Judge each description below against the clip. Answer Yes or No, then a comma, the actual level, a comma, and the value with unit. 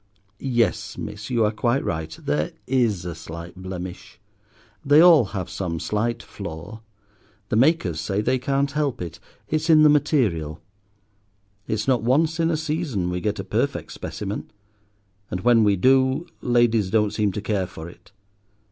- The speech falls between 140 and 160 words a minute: Yes, average, 155 wpm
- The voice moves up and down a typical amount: No, wide, 7.0 semitones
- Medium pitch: No, low, 110 Hz